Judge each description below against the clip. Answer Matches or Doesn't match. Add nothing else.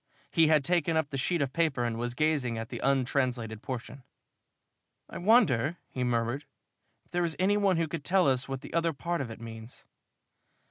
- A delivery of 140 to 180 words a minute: Doesn't match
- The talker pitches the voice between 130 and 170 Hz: Matches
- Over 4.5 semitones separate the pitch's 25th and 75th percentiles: Matches